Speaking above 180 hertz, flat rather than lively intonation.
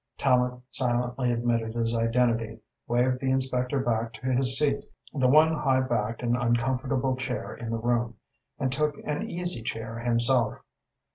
No: low, 125 Hz; narrow, 2.0 semitones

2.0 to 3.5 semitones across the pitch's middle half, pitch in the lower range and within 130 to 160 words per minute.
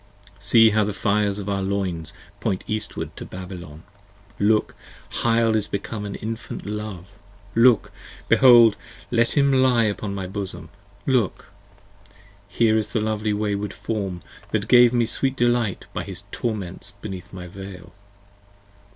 Yes: average, 2.7 semitones; low, 105 Hz; average, 140 wpm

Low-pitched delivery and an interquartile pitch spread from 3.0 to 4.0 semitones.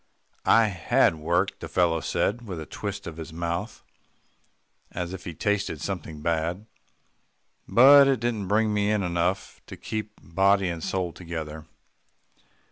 Yes: very low, 90 Hz; average, 3.6 semitones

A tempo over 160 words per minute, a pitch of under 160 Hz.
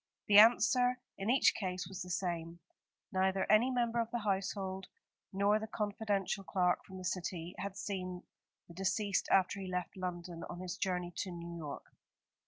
No: average, 170 wpm; high, 190 Hz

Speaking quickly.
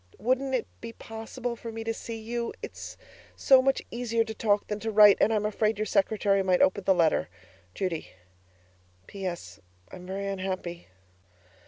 No: average, 165 wpm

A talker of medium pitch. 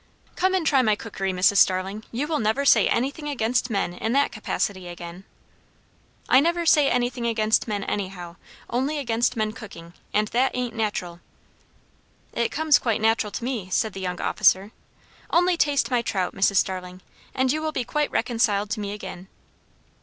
No: high, 225 Hz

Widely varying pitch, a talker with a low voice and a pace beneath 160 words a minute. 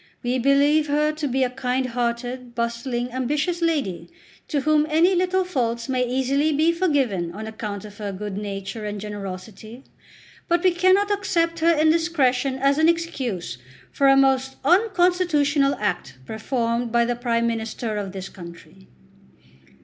No: wide, 5.8 semitones; very high, 260 Hz; average, 150 wpm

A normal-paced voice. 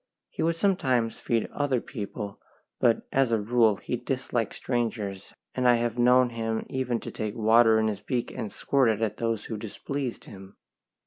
Yes: average, 175 wpm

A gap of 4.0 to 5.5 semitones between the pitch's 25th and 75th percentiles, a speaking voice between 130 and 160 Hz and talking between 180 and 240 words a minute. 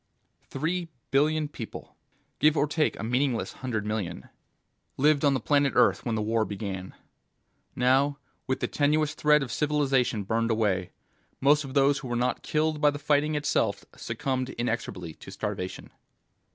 No: average, 4.6 semitones; low, 135 Hz; average, 155 wpm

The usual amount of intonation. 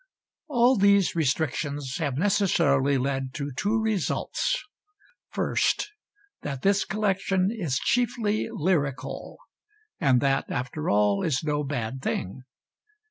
No: wide, 7.0 semitones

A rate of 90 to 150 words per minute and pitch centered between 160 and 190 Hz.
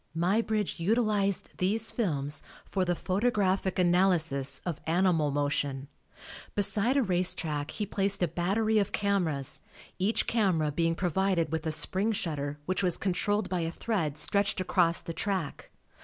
Yes: average, 145 wpm; medium, 185 Hz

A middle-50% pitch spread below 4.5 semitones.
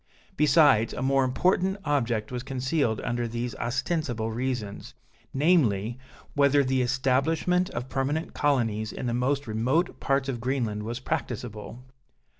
Yes: average, 3.4 semitones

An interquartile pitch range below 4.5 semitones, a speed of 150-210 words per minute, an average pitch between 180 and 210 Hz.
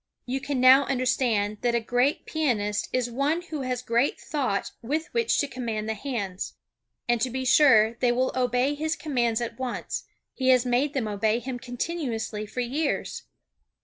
No: average, 3.0 semitones; average, 175 wpm; very high, 250 Hz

